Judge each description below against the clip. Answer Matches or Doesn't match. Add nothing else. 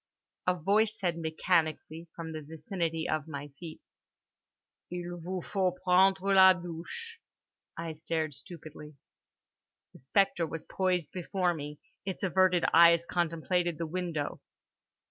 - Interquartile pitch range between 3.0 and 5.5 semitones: Doesn't match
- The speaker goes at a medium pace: Doesn't match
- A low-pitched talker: Doesn't match